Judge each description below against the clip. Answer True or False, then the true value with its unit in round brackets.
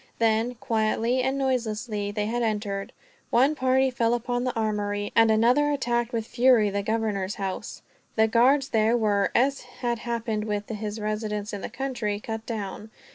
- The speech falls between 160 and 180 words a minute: True (165 wpm)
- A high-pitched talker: True (225 Hz)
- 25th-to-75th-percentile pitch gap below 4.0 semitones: True (2.6 semitones)